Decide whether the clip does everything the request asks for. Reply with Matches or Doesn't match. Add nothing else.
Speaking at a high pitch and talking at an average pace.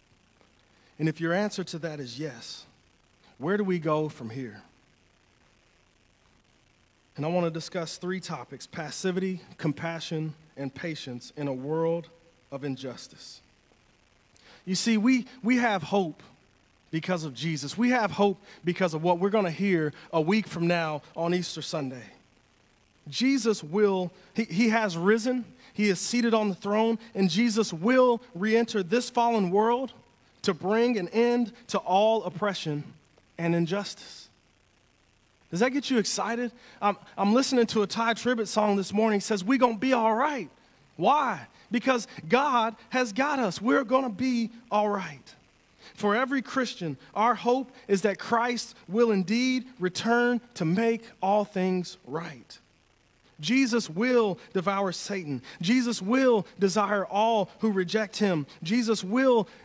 Matches